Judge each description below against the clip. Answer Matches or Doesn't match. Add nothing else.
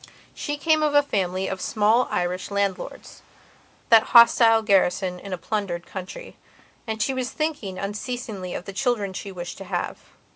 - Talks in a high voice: Matches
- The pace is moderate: Matches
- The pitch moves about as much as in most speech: Matches